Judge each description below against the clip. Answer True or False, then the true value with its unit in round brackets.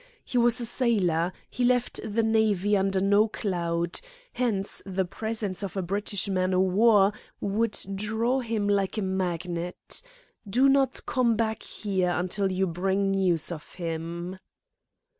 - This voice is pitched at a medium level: False (195 Hz)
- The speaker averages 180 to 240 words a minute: False (145 wpm)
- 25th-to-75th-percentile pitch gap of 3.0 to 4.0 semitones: True (3.3 semitones)